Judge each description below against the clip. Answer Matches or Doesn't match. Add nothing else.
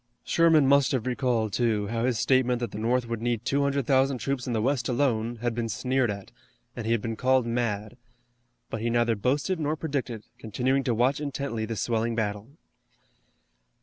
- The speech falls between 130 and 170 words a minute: Doesn't match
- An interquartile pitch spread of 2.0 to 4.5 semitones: Matches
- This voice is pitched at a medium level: Doesn't match